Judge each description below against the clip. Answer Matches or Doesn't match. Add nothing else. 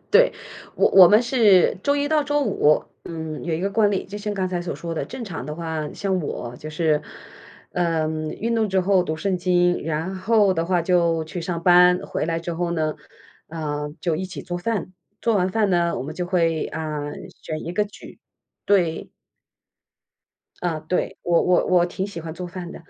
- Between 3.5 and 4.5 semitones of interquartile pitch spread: Doesn't match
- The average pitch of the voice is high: Doesn't match